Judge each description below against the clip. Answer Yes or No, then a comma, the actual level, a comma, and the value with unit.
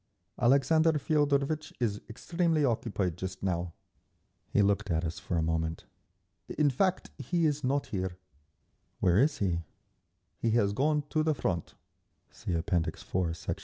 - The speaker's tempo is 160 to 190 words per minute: No, average, 145 wpm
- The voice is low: Yes, low, 110 Hz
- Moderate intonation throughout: No, wide, 8.9 semitones